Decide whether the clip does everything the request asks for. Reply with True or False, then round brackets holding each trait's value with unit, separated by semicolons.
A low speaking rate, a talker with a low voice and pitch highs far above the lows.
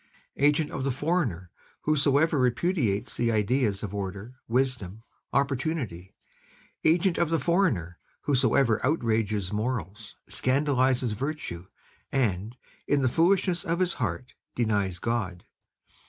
True (110 wpm; 125 Hz; 6.2 semitones)